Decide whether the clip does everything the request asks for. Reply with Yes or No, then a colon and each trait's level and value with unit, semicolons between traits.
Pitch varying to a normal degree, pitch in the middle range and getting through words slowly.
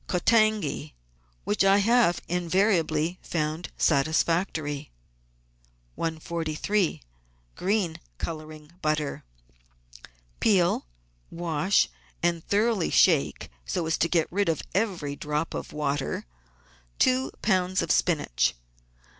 Yes: average, 3.7 semitones; medium, 165 Hz; slow, 95 wpm